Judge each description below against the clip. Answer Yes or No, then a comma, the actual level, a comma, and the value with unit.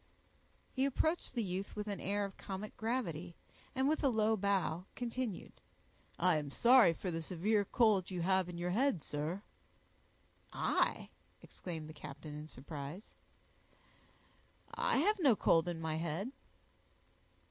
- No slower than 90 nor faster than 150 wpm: Yes, average, 145 wpm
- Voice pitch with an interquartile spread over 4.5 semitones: Yes, wide, 5.5 semitones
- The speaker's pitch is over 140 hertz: Yes, high, 190 Hz